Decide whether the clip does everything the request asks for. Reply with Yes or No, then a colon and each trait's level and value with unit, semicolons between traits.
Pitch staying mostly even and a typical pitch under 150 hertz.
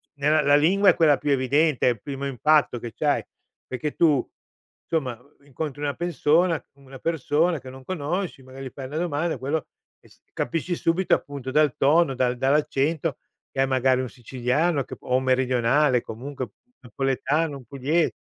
No: average, 3.2 semitones; medium, 140 Hz